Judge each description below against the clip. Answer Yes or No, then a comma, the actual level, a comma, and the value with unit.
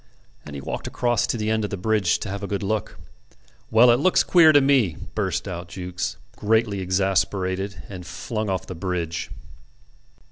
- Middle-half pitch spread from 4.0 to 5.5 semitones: No, average, 3.3 semitones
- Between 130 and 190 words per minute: Yes, average, 180 wpm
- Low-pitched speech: Yes, low, 100 Hz